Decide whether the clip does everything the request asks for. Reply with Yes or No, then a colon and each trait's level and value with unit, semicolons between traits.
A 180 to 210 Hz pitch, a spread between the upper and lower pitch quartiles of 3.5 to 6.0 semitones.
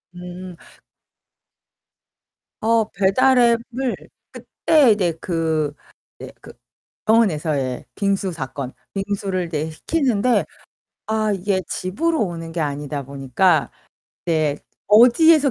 No: high, 190 Hz; wide, 6.4 semitones